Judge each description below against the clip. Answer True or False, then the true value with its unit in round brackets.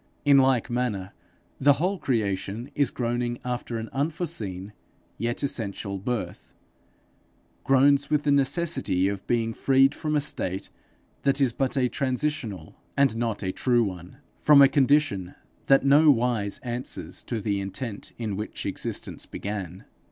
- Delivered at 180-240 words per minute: False (140 wpm)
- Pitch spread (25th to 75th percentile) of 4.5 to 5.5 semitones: True (5.2 semitones)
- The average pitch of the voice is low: True (120 Hz)